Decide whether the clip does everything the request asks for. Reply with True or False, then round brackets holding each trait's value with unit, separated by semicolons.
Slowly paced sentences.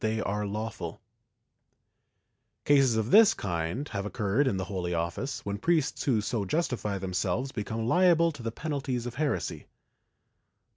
True (130 wpm)